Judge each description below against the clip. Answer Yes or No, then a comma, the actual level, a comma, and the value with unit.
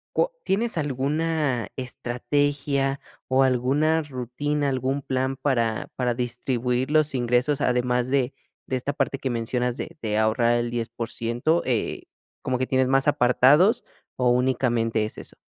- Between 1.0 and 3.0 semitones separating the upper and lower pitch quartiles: Yes, narrow, 2.6 semitones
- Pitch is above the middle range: No, low, 130 Hz